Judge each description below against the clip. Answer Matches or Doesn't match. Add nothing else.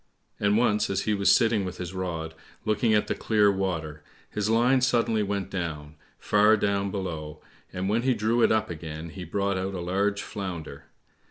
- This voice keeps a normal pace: Matches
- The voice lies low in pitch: Matches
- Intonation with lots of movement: Doesn't match